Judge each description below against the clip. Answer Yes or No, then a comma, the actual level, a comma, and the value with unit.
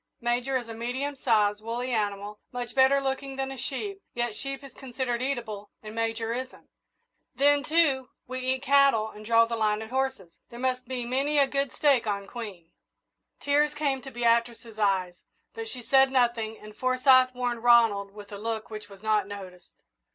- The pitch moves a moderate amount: Yes, average, 3.6 semitones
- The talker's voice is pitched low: No, high, 240 Hz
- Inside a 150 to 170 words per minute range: No, average, 180 wpm